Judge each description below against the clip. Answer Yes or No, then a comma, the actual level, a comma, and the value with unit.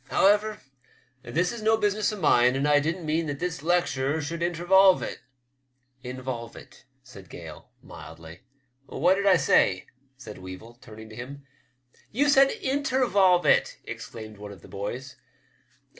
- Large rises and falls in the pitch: Yes, wide, 7.5 semitones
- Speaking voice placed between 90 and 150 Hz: Yes, medium, 140 Hz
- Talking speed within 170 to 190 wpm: Yes, average, 175 wpm